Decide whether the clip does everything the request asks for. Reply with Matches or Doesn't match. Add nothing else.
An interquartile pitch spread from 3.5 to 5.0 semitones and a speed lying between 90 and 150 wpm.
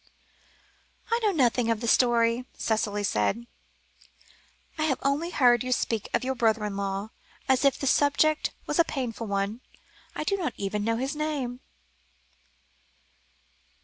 Matches